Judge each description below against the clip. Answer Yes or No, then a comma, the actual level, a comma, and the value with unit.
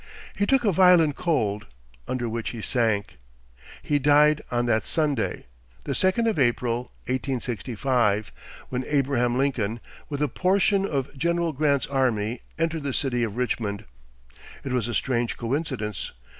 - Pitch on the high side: No, low, 130 Hz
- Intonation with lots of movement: No, average, 4.3 semitones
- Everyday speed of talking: Yes, average, 145 wpm